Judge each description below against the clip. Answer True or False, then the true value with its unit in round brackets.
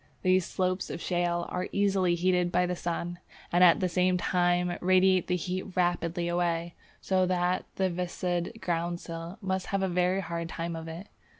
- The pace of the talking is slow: False (175 wpm)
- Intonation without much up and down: True (1.1 semitones)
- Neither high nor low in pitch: True (180 Hz)